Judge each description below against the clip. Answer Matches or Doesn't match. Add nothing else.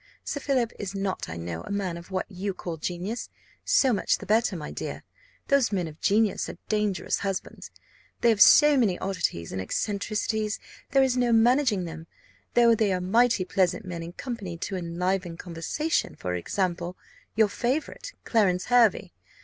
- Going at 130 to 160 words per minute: Doesn't match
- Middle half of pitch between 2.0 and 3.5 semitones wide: Doesn't match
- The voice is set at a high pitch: Matches